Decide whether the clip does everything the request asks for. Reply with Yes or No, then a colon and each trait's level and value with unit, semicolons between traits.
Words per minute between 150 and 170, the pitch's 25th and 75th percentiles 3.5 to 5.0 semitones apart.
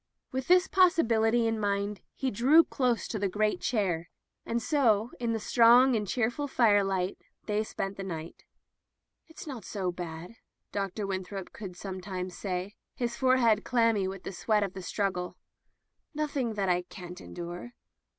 Yes: average, 160 wpm; average, 4.1 semitones